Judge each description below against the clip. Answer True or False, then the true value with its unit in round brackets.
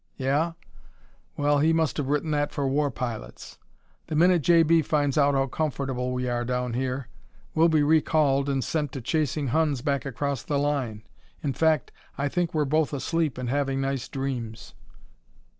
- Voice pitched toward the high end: False (140 Hz)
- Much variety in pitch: False (2.8 semitones)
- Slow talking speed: False (170 wpm)